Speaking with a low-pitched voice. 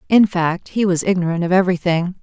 No: medium, 180 Hz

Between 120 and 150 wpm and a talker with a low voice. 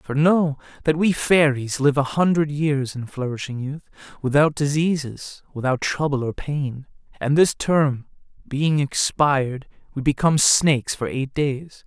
No: average, 145 wpm; medium, 145 Hz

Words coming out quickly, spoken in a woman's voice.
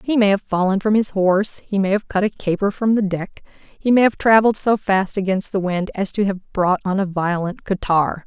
Yes: fast, 240 wpm; female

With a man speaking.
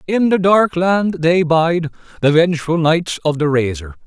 Yes: male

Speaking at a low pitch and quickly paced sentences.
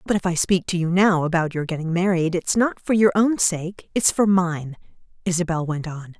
No: medium, 175 Hz; fast, 225 wpm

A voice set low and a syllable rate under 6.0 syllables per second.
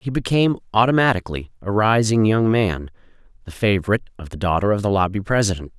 No: low, 105 Hz; 6.5 syllables/s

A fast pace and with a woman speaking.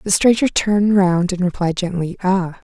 No: average, 175 wpm; female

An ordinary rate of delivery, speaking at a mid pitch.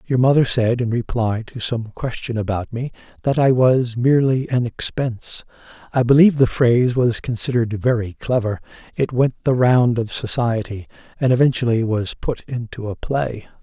No: average, 165 wpm; low, 120 Hz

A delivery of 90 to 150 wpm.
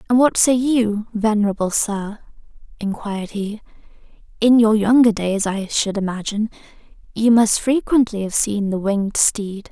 Yes: average, 140 wpm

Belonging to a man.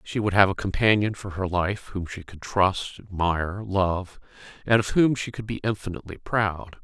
Yes: male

